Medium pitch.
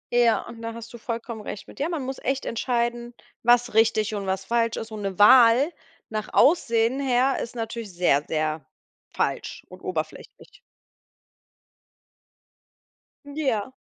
No: high, 230 Hz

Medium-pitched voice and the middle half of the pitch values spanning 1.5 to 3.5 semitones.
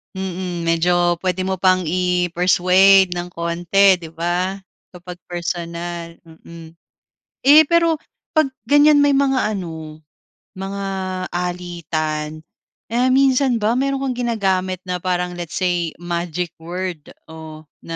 Yes: medium, 180 Hz; narrow, 2.5 semitones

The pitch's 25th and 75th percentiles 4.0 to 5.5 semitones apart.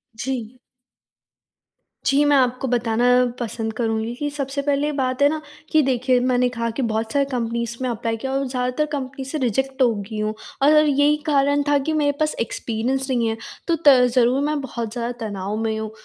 No: average, 3.3 semitones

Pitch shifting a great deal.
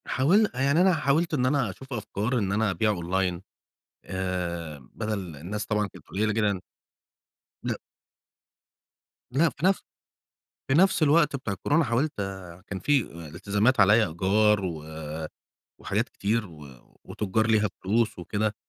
Yes: wide, 5.8 semitones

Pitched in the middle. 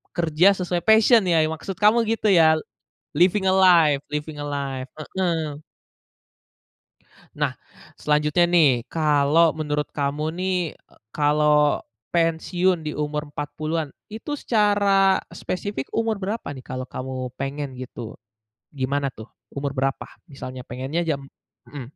Yes: medium, 155 Hz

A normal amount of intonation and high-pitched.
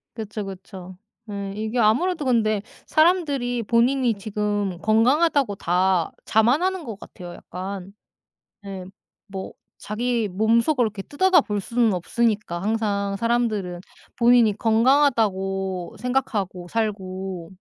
Yes: average, 4.0 semitones; high, 215 Hz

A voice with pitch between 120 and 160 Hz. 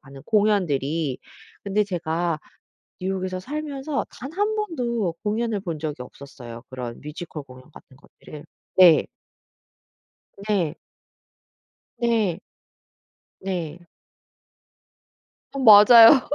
No: medium, 185 Hz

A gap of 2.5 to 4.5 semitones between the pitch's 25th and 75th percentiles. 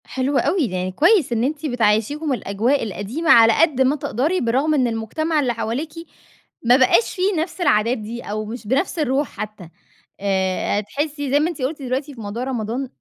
No: average, 5.1 semitones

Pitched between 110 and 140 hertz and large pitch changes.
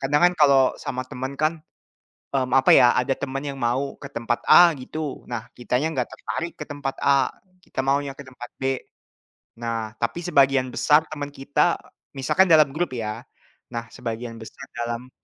No: low, 135 Hz; average, 3.0 semitones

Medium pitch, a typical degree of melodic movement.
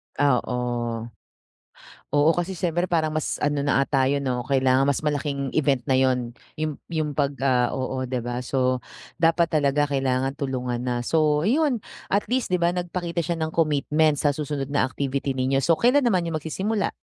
Yes: medium, 145 Hz; average, 3.8 semitones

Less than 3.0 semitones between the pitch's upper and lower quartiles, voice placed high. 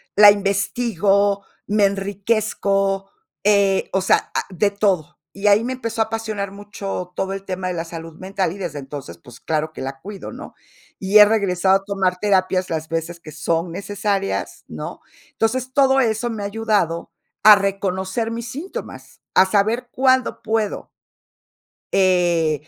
Yes: narrow, 2.6 semitones; high, 195 Hz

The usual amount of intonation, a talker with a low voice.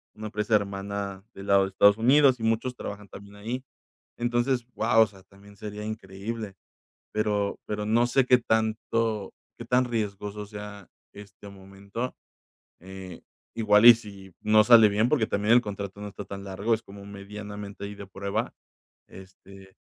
No: narrow, 2.2 semitones; low, 105 Hz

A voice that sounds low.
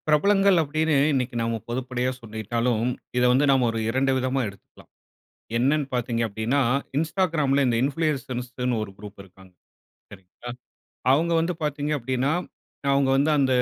Yes: low, 130 Hz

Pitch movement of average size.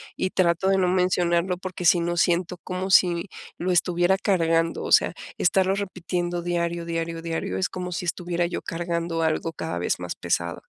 No: narrow, 1.5 semitones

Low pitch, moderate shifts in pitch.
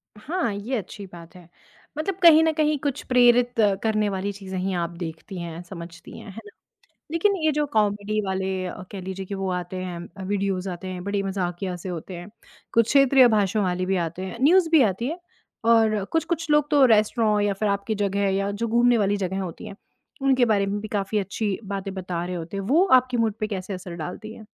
No: high, 200 Hz; average, 4.0 semitones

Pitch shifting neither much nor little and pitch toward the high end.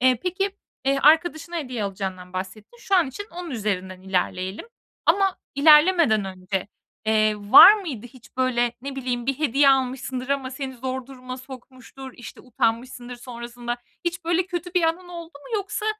No: wide, 5.9 semitones; very high, 260 Hz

